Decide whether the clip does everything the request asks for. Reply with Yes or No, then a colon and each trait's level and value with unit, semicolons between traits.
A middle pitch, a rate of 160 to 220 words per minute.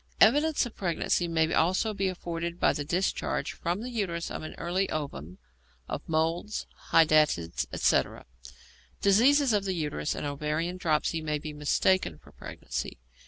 No: medium, 170 Hz; average, 150 wpm